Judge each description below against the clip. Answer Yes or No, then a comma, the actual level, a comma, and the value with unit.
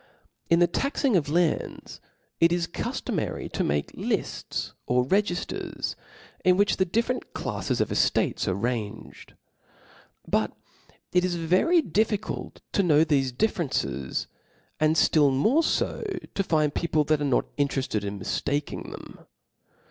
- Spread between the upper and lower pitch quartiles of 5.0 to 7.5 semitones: Yes, wide, 5.4 semitones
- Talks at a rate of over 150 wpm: No, slow, 135 wpm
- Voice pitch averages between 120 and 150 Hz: No, medium, 160 Hz